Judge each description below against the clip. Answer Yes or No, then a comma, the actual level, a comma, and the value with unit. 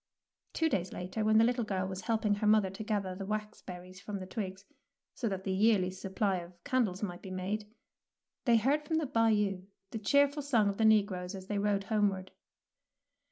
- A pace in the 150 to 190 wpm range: No, average, 200 wpm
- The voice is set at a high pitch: Yes, high, 205 Hz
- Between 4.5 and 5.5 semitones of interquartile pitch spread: No, average, 2.8 semitones